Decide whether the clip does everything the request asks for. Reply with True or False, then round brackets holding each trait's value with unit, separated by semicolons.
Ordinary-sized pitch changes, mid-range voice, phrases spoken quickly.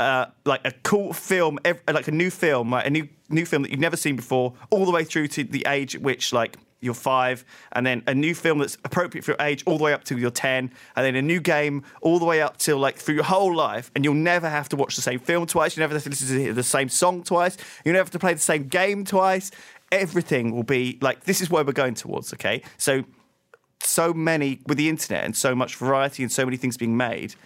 True (4.4 semitones; 150 Hz; 260 wpm)